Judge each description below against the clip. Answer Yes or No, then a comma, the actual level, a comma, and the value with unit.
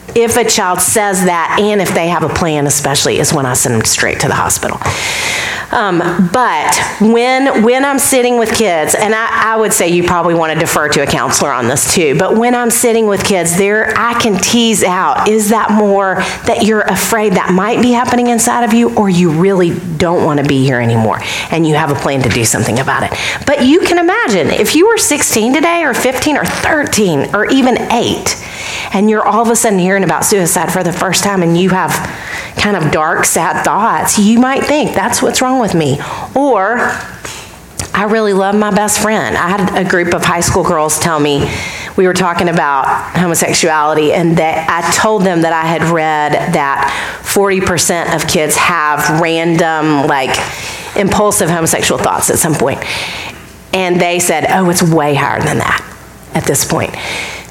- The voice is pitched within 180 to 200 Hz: Yes, medium, 185 Hz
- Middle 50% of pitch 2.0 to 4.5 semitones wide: No, average, 5.2 semitones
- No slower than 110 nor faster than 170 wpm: No, average, 200 wpm